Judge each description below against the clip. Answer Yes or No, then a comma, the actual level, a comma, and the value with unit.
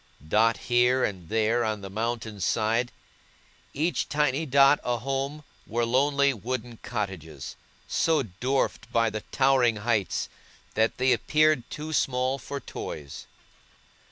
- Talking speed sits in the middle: No, slow, 130 wpm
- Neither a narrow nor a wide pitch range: Yes, average, 3.9 semitones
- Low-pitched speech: Yes, low, 120 Hz